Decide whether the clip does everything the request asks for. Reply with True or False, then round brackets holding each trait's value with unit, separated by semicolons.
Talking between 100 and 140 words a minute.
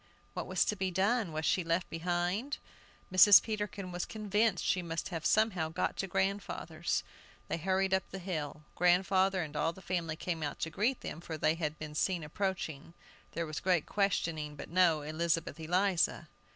False (180 wpm)